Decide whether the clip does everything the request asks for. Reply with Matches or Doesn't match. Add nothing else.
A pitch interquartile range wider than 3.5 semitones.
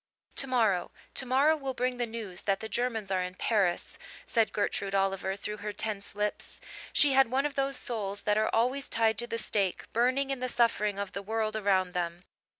Matches